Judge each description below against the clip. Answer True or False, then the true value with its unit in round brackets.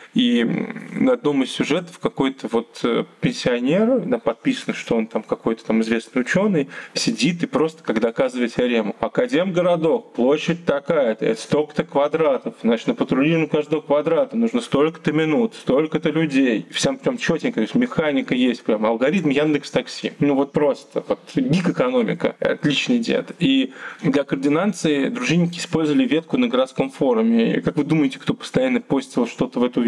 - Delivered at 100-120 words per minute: False (160 wpm)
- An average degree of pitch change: False (8.9 semitones)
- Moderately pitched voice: True (170 Hz)